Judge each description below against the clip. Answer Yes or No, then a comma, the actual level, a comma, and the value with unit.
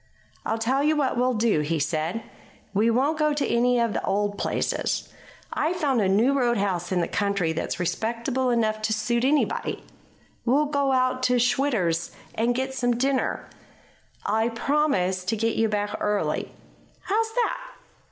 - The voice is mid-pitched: No, high, 235 Hz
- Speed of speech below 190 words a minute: Yes, average, 160 wpm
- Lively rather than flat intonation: No, average, 4.5 semitones